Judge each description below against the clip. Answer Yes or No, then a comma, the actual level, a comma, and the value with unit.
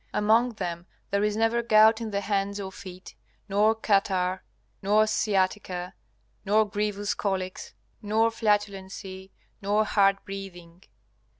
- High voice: Yes, high, 200 Hz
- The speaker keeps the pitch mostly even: Yes, narrow, 2.1 semitones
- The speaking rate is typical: No, slow, 120 wpm